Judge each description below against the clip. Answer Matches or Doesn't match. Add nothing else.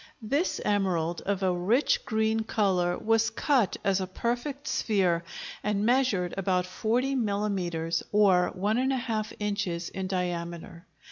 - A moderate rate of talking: Doesn't match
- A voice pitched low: Doesn't match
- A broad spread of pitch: Doesn't match